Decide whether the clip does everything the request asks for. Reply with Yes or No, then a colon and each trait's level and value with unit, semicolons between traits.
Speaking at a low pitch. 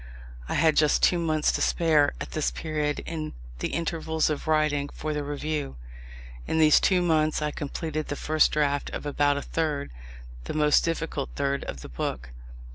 No: medium, 155 Hz